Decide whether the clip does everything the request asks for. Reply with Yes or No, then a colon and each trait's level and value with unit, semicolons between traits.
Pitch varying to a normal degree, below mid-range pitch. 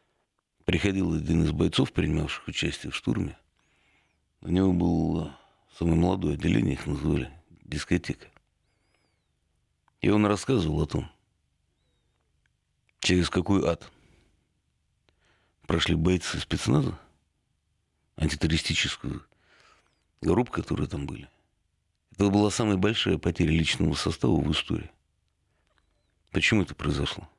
Yes: average, 3.5 semitones; very low, 85 Hz